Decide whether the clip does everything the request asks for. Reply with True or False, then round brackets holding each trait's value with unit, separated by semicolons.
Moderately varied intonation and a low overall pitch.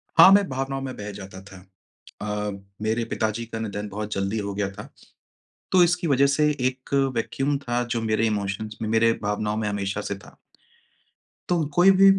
True (4.7 semitones; 110 Hz)